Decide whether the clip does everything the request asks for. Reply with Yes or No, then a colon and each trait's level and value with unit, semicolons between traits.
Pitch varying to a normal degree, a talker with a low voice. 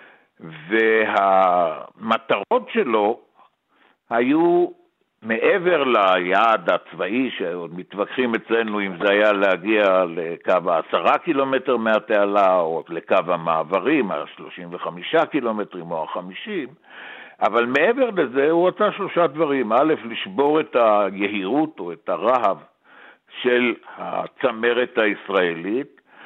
No: wide, 8.3 semitones; low, 125 Hz